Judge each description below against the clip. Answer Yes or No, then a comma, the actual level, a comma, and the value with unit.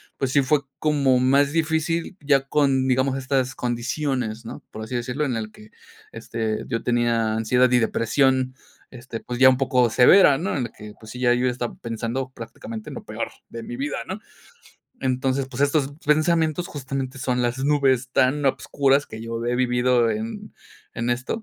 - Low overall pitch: Yes, low, 130 Hz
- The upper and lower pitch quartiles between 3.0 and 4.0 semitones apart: No, narrow, 2.6 semitones